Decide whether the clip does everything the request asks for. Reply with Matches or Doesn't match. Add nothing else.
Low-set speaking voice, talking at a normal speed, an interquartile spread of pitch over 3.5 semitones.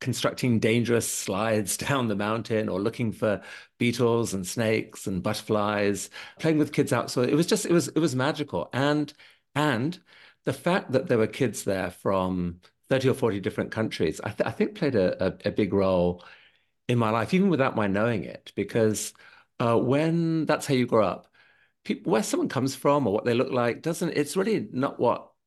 Matches